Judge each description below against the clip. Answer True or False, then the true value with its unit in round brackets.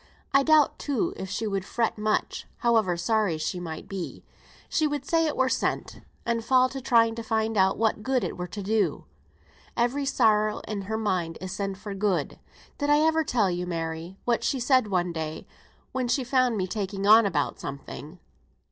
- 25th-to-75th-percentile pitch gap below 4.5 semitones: False (5.1 semitones)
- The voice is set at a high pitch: True (215 Hz)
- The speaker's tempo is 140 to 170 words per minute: False (190 wpm)